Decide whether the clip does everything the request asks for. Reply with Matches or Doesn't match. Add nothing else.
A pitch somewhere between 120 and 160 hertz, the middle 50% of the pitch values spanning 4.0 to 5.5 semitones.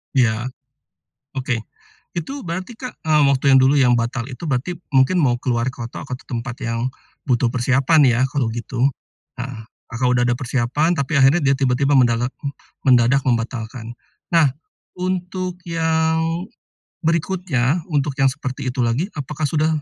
Matches